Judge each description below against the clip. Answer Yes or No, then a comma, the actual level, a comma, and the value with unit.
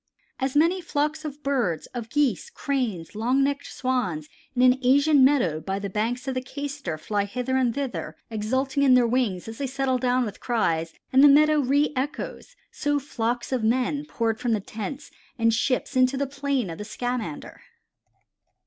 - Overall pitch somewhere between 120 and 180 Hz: No, very high, 255 Hz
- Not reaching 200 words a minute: Yes, average, 175 wpm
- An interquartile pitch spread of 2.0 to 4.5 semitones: Yes, average, 3.9 semitones